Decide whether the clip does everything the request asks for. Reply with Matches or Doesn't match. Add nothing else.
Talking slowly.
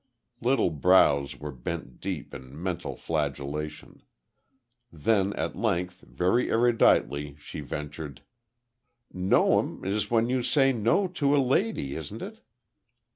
Matches